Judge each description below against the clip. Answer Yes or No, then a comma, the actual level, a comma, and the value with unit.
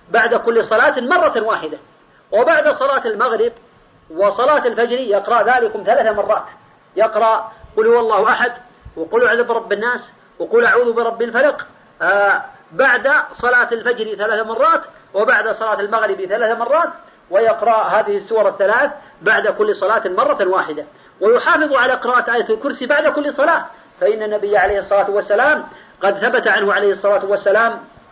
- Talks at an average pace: No, fast, 140 wpm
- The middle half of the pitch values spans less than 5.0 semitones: No, wide, 5.5 semitones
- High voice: Yes, high, 235 Hz